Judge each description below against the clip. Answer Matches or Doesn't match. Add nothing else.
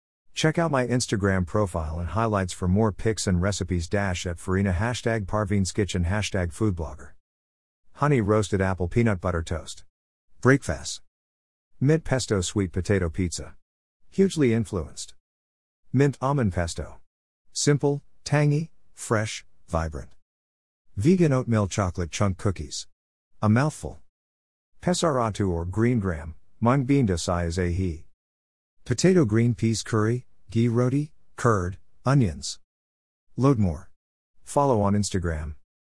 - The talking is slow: Matches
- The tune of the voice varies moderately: Doesn't match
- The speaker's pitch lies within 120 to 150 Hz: Doesn't match